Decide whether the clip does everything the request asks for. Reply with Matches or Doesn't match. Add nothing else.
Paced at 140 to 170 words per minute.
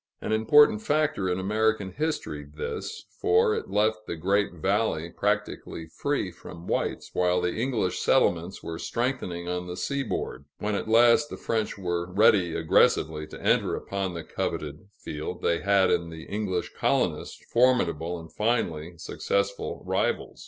Matches